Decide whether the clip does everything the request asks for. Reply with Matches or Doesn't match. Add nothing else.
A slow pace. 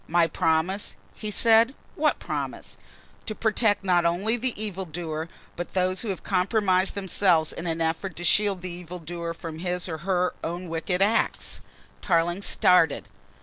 Doesn't match